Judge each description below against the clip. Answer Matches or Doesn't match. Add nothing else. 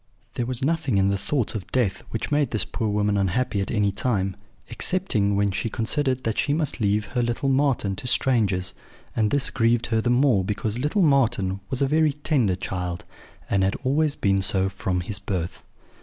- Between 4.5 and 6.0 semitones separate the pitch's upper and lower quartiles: Matches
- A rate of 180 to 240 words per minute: Matches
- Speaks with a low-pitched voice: Matches